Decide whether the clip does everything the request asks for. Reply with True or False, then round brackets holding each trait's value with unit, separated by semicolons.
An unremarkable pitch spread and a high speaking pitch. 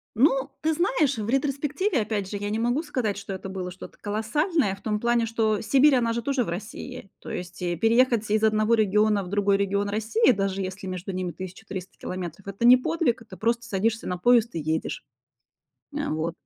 True (3.9 semitones; 215 Hz)